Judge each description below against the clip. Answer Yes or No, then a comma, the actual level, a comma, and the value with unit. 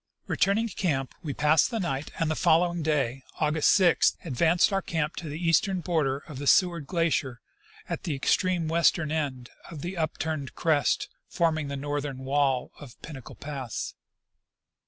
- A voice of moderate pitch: Yes, medium, 155 Hz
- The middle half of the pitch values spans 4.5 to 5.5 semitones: No, average, 3.4 semitones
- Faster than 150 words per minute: Yes, average, 160 wpm